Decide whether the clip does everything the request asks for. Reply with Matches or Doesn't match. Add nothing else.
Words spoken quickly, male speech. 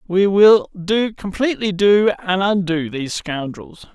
Doesn't match